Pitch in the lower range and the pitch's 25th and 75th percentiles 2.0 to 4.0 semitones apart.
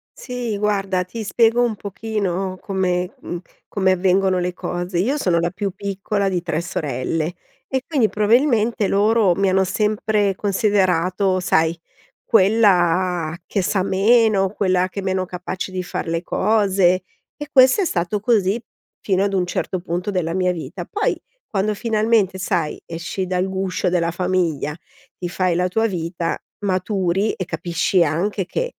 No: high, 190 Hz; average, 2.7 semitones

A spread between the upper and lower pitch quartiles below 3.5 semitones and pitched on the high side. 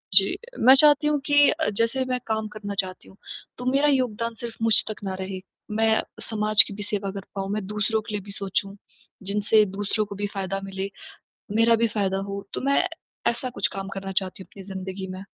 Yes: average, 2.9 semitones; high, 210 Hz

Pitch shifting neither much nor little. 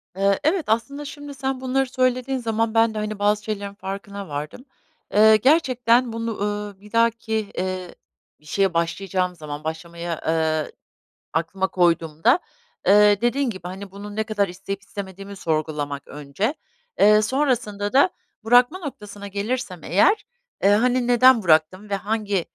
Yes: average, 4.3 semitones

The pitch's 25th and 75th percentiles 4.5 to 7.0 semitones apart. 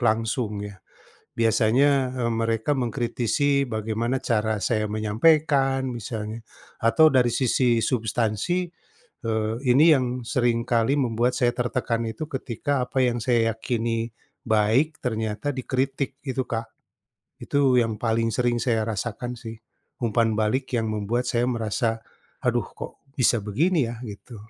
No: average, 2.7 semitones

